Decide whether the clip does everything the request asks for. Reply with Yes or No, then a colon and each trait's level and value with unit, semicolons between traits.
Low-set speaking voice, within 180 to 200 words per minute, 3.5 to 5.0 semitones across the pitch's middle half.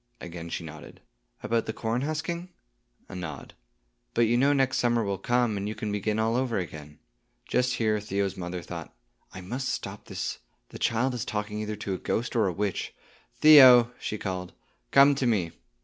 Yes: low, 110 Hz; average, 185 wpm; average, 4.4 semitones